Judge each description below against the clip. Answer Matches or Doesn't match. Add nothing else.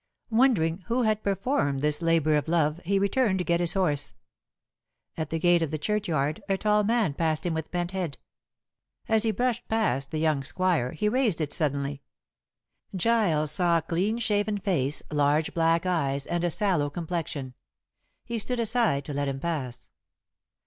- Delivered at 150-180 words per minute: Matches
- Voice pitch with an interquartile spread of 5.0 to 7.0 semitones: Matches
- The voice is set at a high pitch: Doesn't match